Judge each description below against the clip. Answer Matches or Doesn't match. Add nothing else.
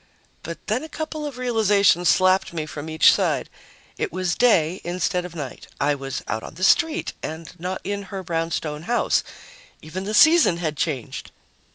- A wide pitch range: Doesn't match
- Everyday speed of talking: Matches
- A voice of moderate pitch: Matches